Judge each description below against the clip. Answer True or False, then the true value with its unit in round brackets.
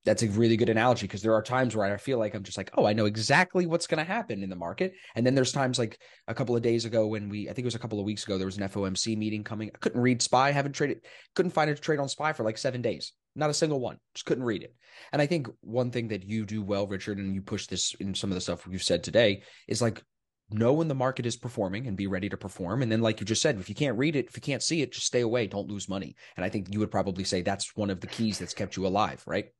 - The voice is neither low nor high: False (110 Hz)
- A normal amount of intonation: True (4.3 semitones)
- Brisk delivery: True (310 wpm)